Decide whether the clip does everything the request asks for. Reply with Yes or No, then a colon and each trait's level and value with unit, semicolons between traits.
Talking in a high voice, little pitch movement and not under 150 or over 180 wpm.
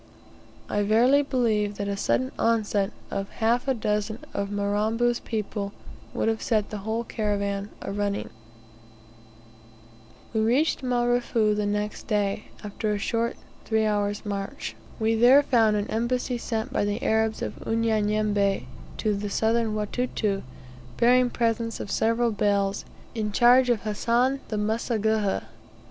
No: high, 220 Hz; narrow, 2.3 semitones; slow, 135 wpm